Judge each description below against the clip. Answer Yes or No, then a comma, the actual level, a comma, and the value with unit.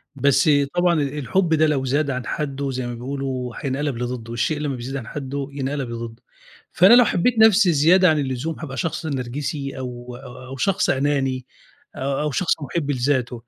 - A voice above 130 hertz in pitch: Yes, medium, 140 Hz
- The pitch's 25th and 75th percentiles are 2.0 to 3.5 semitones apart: Yes, average, 3.0 semitones